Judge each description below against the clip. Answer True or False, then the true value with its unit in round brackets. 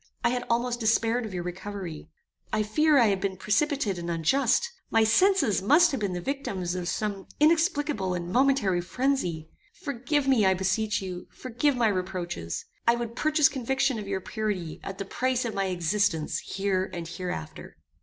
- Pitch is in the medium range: False (210 Hz)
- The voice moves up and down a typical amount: False (5.9 semitones)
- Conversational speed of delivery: True (175 wpm)